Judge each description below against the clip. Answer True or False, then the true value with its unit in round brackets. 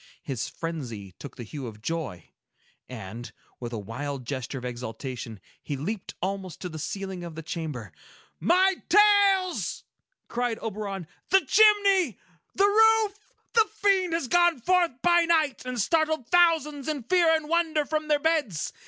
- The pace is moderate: True (155 wpm)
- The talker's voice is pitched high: True (245 Hz)